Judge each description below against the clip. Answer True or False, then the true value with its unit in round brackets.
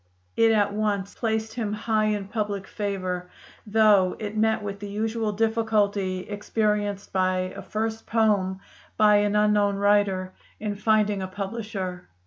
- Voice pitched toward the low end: False (205 Hz)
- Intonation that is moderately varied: False (1.6 semitones)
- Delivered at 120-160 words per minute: True (140 wpm)